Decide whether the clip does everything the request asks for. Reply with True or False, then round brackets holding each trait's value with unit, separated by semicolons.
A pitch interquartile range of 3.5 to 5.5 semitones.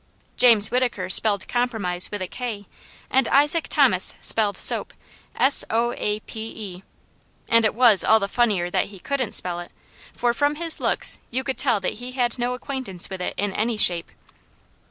True (3.8 semitones)